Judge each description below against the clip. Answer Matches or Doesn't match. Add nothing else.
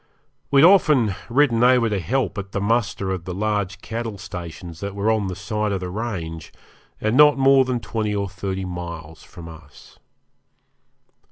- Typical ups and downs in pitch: Matches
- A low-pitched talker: Matches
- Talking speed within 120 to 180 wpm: Matches